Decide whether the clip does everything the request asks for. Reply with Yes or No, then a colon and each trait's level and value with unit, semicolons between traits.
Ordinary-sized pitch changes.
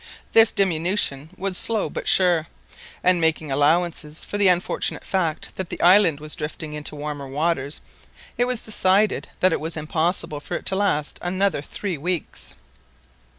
Yes: average, 4.0 semitones